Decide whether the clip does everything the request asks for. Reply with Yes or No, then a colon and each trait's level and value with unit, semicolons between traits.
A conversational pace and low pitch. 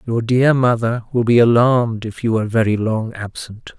Yes: average, 190 wpm; low, 115 Hz